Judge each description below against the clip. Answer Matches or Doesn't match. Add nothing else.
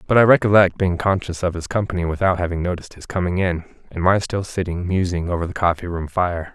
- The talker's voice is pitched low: Matches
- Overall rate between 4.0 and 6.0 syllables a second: Doesn't match